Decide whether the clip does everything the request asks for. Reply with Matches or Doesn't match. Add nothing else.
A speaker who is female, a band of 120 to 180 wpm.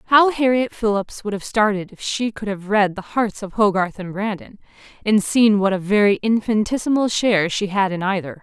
Doesn't match